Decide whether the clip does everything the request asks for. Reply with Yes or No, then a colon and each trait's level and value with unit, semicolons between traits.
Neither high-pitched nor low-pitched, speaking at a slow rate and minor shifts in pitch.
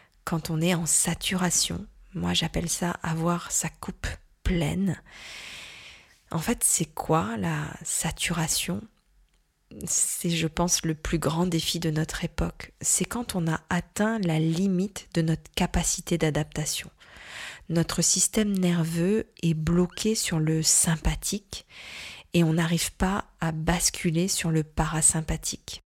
Yes: medium, 170 Hz; slow, 130 wpm; narrow, 2.0 semitones